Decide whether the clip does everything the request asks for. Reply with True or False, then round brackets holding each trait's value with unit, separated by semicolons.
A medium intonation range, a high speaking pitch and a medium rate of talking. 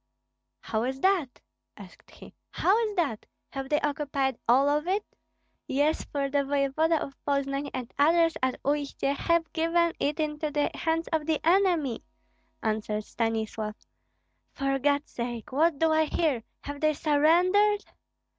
True (3.1 semitones; 290 Hz; 145 wpm)